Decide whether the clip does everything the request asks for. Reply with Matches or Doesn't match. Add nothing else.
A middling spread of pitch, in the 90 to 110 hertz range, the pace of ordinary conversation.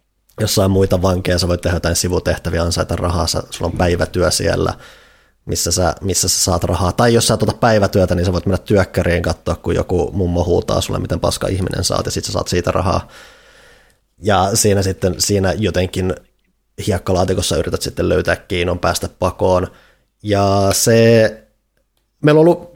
Doesn't match